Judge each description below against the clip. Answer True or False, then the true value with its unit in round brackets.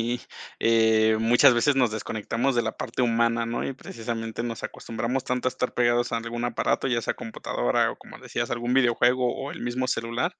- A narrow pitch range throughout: True (1.4 semitones)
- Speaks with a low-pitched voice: True (120 Hz)